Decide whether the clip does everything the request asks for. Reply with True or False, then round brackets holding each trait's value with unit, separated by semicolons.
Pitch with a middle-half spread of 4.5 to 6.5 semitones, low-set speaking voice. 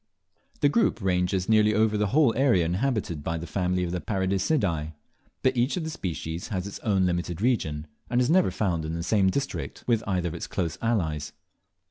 True (5.1 semitones; 95 Hz)